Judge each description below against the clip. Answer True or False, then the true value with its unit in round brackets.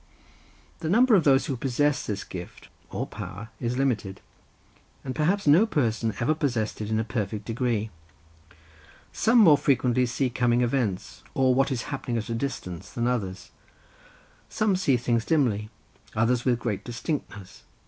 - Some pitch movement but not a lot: True (4.0 semitones)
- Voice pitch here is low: True (125 Hz)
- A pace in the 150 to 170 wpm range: True (155 wpm)